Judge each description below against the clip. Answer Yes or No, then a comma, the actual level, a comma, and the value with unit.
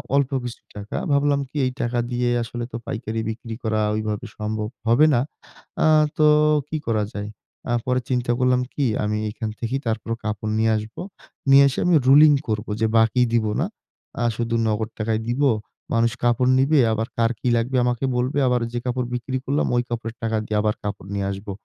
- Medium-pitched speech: No, low, 115 Hz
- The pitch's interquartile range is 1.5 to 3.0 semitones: Yes, narrow, 2.6 semitones